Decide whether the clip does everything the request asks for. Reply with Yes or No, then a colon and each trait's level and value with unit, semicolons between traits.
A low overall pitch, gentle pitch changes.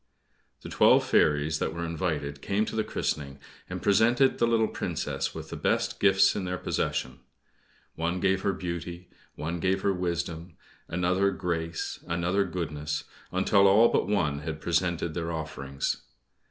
No: very low, 85 Hz; average, 3.2 semitones